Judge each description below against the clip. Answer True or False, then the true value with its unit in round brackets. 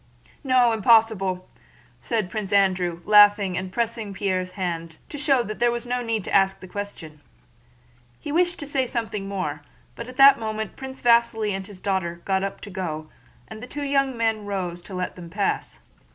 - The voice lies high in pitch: True (205 Hz)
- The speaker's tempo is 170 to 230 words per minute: True (185 wpm)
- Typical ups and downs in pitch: True (4.1 semitones)